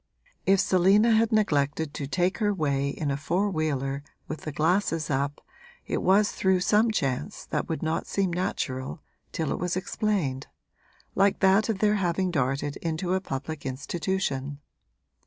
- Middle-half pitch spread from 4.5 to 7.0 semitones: Yes, average, 5.2 semitones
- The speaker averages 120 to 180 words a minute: Yes, average, 155 wpm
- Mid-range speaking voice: Yes, medium, 170 Hz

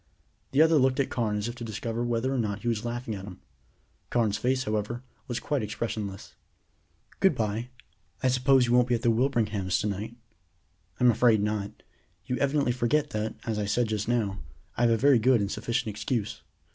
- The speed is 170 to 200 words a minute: Yes, average, 195 wpm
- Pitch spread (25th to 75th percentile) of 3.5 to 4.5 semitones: No, average, 2.8 semitones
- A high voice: No, low, 115 Hz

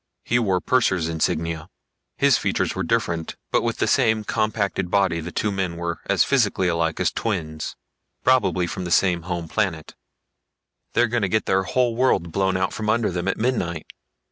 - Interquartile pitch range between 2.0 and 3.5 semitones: No, average, 4.3 semitones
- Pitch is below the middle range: Yes, very low, 95 Hz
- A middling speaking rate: Yes, average, 175 wpm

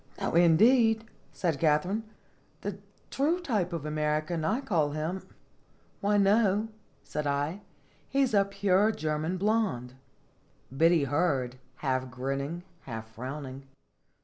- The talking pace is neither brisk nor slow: No, slow, 120 wpm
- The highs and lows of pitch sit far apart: Yes, wide, 6.0 semitones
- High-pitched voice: No, medium, 165 Hz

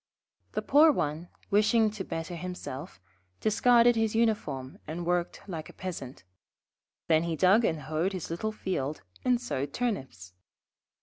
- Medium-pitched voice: Yes, medium, 180 Hz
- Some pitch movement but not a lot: No, wide, 5.9 semitones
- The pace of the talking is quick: No, average, 140 wpm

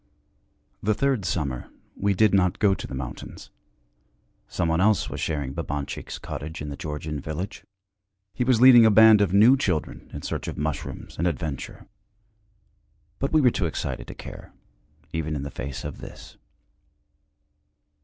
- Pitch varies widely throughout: Yes, wide, 6.5 semitones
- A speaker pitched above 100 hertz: No, very low, 85 Hz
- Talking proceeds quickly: No, average, 165 wpm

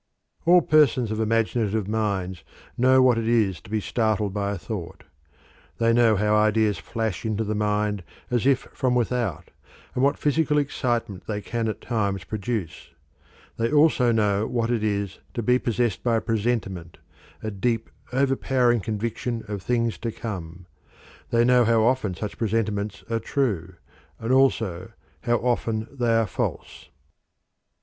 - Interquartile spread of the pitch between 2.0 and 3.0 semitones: Yes, average, 2.7 semitones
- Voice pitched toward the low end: Yes, low, 110 Hz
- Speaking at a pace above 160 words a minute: No, average, 155 wpm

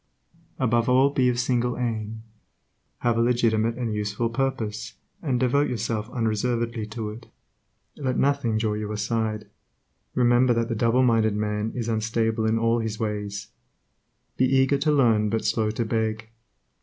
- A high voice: No, low, 115 Hz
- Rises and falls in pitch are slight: Yes, narrow, 2.1 semitones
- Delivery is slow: No, average, 150 wpm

